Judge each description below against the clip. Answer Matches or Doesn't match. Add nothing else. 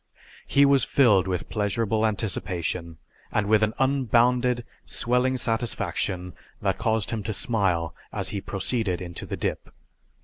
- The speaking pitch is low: Matches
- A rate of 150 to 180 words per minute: Doesn't match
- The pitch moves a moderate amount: Matches